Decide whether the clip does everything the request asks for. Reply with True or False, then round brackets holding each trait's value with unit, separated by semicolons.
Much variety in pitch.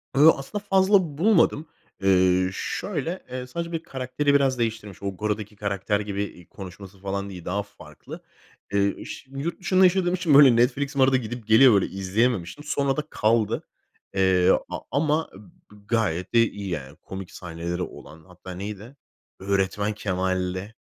True (6.6 semitones)